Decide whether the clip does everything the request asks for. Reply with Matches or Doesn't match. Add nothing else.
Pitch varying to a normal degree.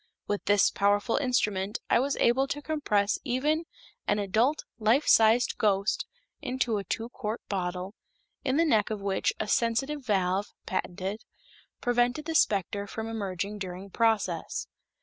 Matches